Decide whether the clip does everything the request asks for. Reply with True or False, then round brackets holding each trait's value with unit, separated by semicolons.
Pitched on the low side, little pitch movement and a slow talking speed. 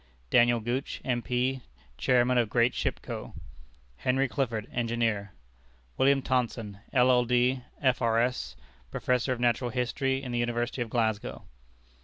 True (120 Hz; 1.5 semitones; 120 wpm)